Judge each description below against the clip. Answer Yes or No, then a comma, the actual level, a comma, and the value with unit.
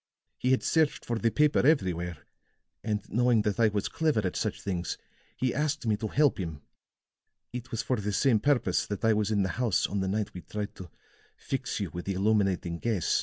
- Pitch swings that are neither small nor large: Yes, average, 4.5 semitones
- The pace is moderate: No, fast, 210 wpm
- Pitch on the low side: Yes, low, 105 Hz